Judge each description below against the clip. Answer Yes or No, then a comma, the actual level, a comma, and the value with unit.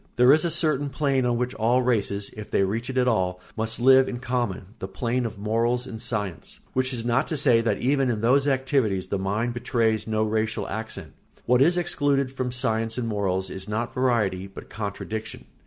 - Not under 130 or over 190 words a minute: No, fast, 205 wpm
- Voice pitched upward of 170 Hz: No, low, 115 Hz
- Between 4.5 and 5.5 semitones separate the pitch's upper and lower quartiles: No, average, 3.3 semitones